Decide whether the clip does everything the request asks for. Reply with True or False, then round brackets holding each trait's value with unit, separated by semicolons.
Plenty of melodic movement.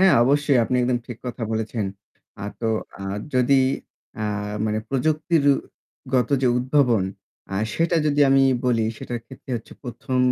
False (3.2 semitones)